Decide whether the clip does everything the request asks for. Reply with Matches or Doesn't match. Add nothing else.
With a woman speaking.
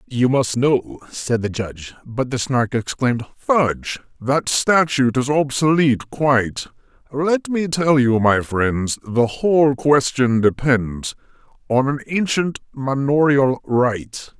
Doesn't match